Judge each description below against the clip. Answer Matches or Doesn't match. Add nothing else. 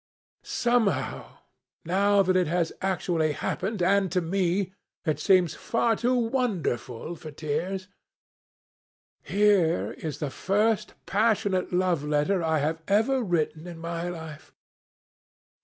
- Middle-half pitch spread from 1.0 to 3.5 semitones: Doesn't match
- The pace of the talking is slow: Matches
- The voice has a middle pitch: Matches